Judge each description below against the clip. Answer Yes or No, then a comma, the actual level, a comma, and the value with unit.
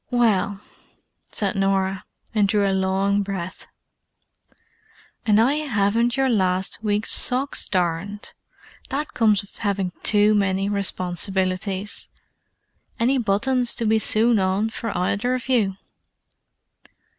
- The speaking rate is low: Yes, slow, 115 wpm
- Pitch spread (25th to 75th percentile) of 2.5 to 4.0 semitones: Yes, average, 2.9 semitones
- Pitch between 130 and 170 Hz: No, high, 205 Hz